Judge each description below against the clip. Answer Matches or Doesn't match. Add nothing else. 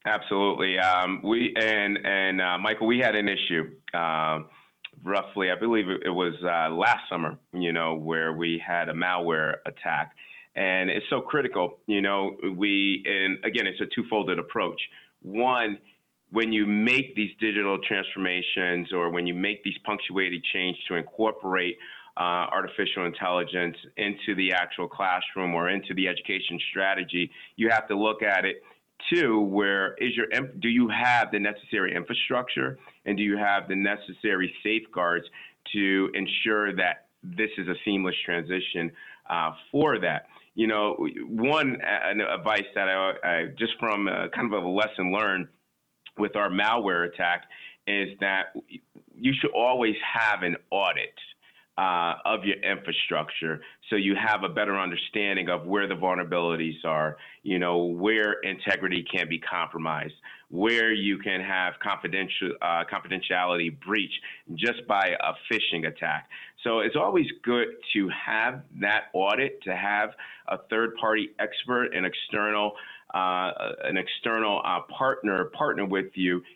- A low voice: Matches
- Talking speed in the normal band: Matches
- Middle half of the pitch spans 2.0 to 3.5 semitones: Matches